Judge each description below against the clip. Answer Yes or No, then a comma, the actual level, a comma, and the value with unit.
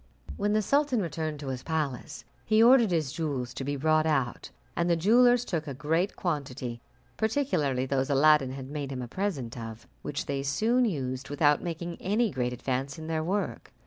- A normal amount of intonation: No, wide, 5.9 semitones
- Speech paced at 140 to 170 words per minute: No, average, 185 wpm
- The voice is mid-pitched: Yes, medium, 150 Hz